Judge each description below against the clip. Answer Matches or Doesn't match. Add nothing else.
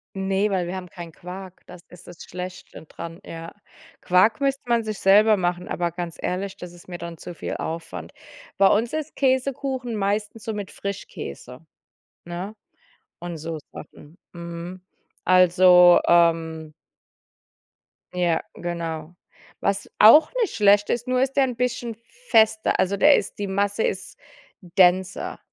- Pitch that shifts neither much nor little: Matches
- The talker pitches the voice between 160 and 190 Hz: Matches